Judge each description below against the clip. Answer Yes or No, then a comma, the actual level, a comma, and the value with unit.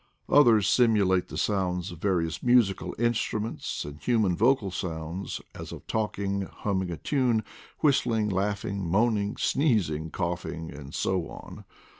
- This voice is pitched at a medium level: No, low, 100 Hz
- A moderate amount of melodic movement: Yes, average, 4.0 semitones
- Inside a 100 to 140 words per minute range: Yes, slow, 135 wpm